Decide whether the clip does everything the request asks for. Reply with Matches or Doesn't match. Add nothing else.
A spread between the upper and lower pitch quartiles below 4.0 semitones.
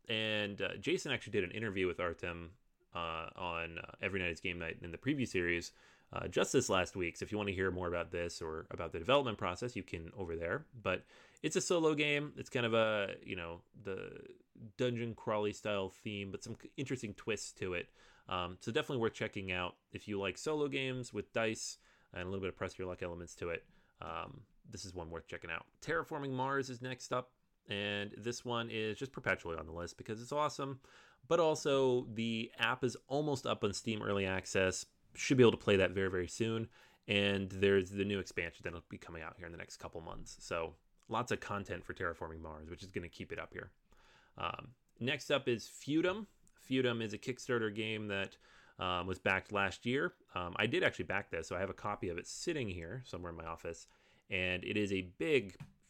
Doesn't match